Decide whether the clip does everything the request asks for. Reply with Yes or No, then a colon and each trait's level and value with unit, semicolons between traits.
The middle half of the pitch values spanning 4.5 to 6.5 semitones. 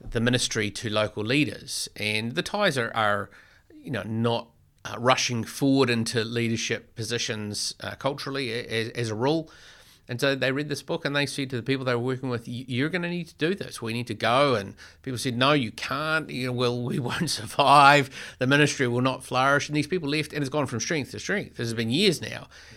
No: average, 3.4 semitones